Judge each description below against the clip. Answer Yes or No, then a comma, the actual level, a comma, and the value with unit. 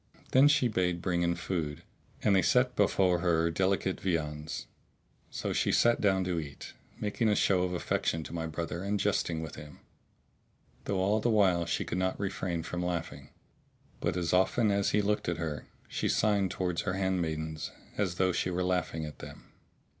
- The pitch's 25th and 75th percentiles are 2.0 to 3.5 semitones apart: Yes, average, 3.0 semitones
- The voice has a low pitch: Yes, very low, 90 Hz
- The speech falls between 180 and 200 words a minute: Yes, average, 185 wpm